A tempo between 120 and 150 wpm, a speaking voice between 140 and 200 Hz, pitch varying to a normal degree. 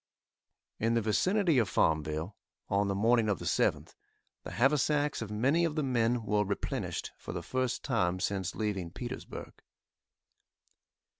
No: average, 145 wpm; low, 115 Hz; average, 4.8 semitones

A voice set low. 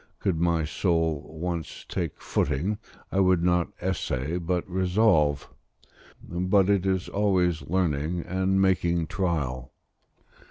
Yes: very low, 90 Hz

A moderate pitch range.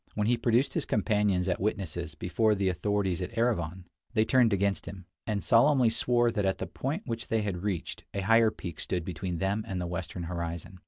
Yes: average, 4.1 semitones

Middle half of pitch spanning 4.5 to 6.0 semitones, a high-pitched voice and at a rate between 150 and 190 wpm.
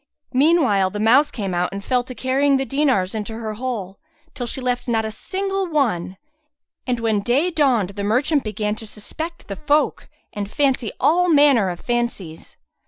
Yes: wide, 5.4 semitones; high, 240 Hz; average, 175 wpm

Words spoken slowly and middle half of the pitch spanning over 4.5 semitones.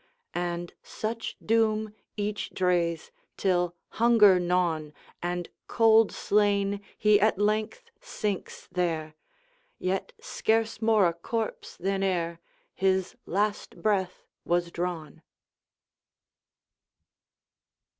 No: slow, 80 wpm; average, 3.7 semitones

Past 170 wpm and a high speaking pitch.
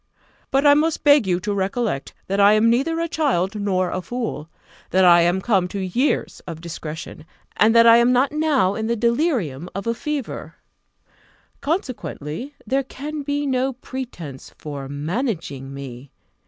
No: average, 165 wpm; high, 220 Hz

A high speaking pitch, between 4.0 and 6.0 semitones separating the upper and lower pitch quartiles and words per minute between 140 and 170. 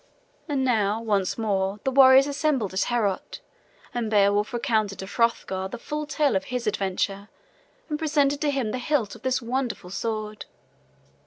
Yes: high, 230 Hz; average, 4.9 semitones; average, 160 wpm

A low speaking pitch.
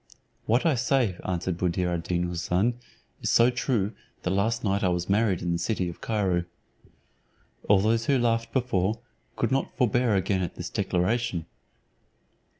Yes: low, 100 Hz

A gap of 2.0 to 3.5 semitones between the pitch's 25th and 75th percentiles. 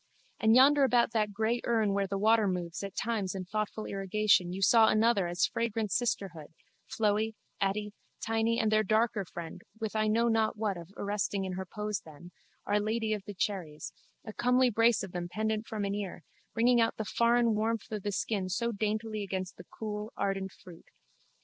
Yes: narrow, 2.5 semitones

